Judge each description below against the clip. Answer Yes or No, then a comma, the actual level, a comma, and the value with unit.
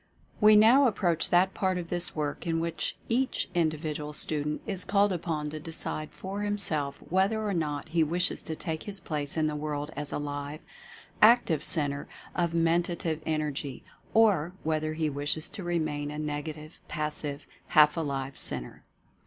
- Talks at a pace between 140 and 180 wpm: Yes, average, 165 wpm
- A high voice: No, medium, 160 Hz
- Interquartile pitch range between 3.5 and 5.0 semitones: No, average, 3.1 semitones